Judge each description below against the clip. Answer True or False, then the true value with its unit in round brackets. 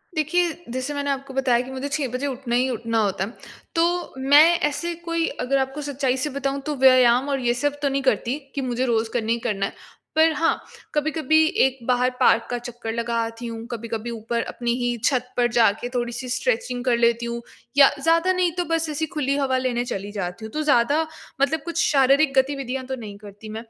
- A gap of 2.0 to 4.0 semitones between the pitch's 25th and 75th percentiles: True (3.3 semitones)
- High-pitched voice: True (260 Hz)